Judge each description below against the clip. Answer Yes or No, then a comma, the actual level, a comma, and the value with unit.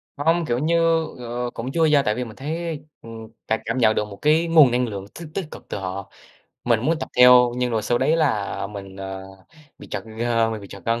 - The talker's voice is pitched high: No, low, 120 Hz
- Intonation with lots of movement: Yes, wide, 5.9 semitones